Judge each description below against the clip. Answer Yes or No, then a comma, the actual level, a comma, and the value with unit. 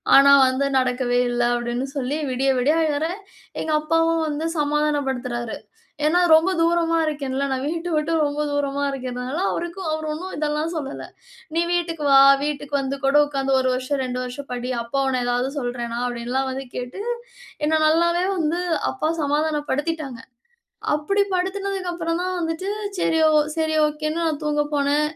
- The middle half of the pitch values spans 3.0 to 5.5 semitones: Yes, average, 3.7 semitones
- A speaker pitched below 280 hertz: No, very high, 295 Hz